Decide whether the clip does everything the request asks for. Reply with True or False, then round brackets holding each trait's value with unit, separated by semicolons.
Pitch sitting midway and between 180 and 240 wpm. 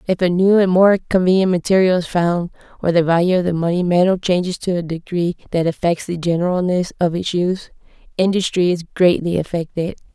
True (175 Hz; 185 wpm)